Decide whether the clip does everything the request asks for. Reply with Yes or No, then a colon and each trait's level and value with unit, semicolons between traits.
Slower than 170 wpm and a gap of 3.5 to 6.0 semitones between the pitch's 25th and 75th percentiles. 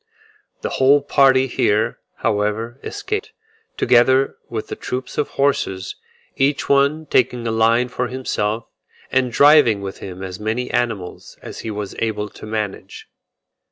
Yes: average, 140 wpm; average, 3.9 semitones